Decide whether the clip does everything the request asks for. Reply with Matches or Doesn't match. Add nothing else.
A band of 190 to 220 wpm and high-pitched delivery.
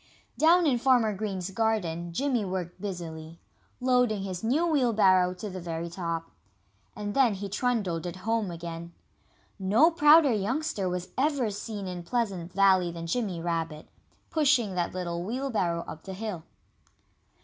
Doesn't match